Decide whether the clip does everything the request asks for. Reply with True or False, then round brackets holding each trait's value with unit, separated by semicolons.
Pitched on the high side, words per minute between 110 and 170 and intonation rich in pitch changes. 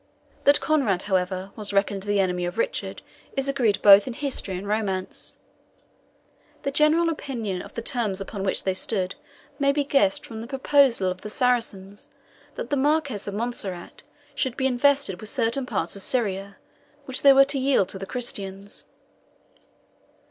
True (220 Hz; 165 wpm; 5.8 semitones)